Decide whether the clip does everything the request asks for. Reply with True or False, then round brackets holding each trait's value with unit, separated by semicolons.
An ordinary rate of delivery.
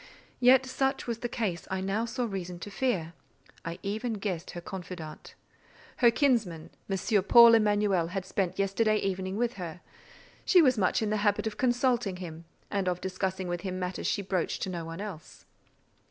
True (185 wpm)